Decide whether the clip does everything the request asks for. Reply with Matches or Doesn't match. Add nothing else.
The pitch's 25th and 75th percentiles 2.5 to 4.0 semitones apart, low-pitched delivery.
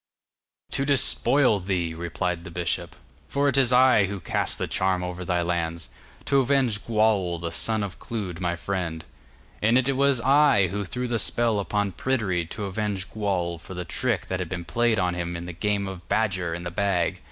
Doesn't match